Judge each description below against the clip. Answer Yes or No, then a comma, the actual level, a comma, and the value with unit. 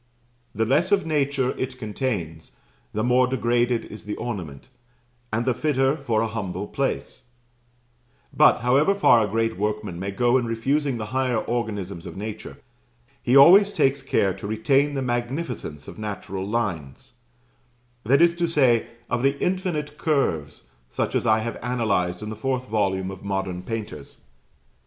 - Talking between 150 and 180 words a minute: Yes, average, 155 wpm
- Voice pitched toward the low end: Yes, low, 120 Hz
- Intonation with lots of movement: No, average, 4.5 semitones